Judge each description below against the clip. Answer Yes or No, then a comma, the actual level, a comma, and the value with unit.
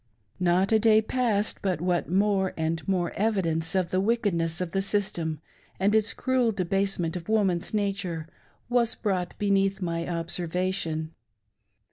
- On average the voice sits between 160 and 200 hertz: Yes, high, 190 Hz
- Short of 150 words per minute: Yes, average, 140 wpm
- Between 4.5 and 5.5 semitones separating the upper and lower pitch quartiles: No, average, 3.2 semitones